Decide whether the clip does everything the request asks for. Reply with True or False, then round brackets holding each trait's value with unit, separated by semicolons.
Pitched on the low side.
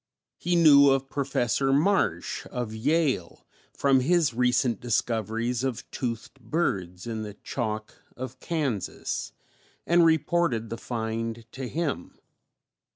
True (125 Hz)